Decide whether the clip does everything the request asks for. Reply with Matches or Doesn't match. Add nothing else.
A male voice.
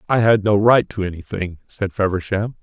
Matches